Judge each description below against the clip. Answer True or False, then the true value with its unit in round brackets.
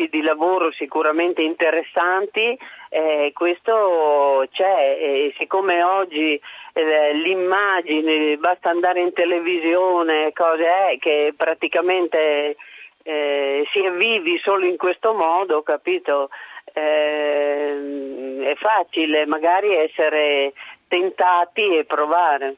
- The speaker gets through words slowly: True (95 wpm)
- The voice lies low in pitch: False (160 Hz)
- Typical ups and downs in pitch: True (3.3 semitones)